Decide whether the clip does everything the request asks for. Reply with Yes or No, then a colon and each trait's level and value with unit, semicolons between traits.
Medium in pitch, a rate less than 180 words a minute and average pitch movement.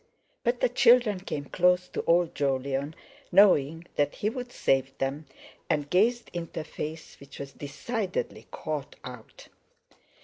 No: medium, 160 Hz; average, 145 wpm; wide, 6.2 semitones